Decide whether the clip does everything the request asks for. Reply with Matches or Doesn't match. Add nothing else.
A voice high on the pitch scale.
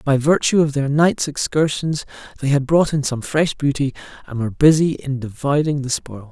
Doesn't match